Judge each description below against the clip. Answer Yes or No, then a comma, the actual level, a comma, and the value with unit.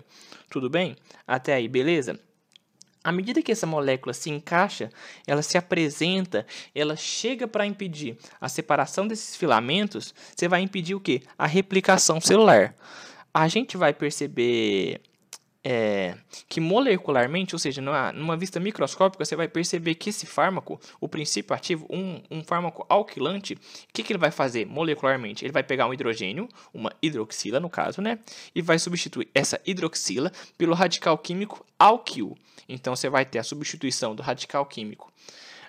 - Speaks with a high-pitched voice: No, medium, 165 Hz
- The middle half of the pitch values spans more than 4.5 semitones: Yes, average, 5.0 semitones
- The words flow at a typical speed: Yes, average, 155 wpm